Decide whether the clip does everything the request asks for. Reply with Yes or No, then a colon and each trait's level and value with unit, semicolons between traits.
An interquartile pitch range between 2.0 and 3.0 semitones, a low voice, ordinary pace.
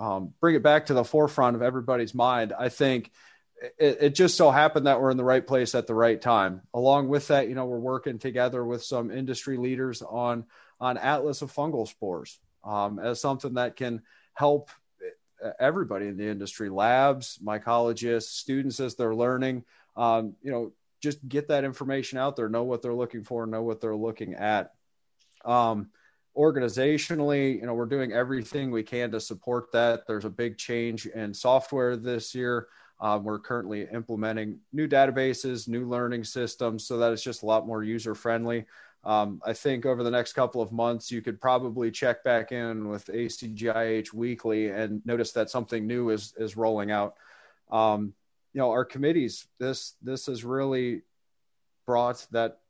Yes: average, 2.7 semitones; low, 120 Hz; average, 180 wpm